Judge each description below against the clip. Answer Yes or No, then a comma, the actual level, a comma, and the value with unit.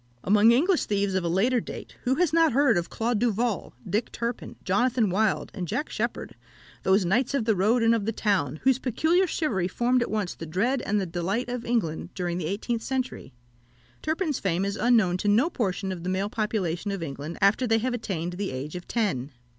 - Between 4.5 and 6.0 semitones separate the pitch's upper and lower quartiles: Yes, average, 4.9 semitones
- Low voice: No, high, 210 Hz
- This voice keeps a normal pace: No, fast, 210 wpm